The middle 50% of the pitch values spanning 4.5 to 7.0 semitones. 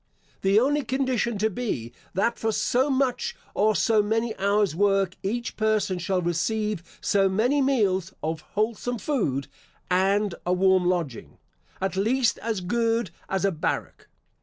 No: average, 3.7 semitones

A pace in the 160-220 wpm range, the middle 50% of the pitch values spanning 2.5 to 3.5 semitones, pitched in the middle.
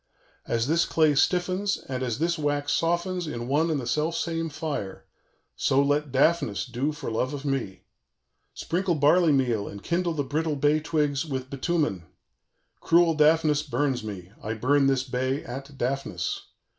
No: average, 165 wpm; average, 3.9 semitones; medium, 145 Hz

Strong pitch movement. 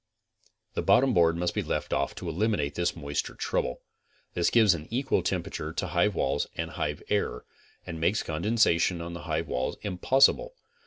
No: average, 4.6 semitones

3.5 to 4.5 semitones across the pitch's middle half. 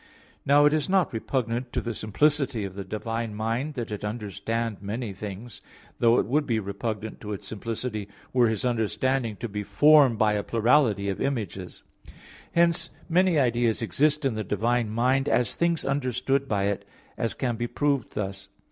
Yes: average, 4.2 semitones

